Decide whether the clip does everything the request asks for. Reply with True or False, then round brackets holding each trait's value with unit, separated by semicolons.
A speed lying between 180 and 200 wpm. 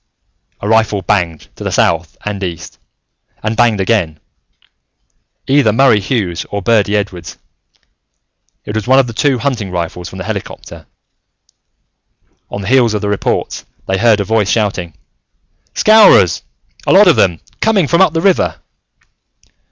False (150 wpm)